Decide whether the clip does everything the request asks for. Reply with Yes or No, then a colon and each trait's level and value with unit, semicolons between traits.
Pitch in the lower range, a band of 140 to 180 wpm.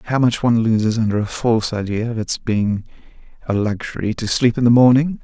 No: low, 115 Hz; fast, 205 wpm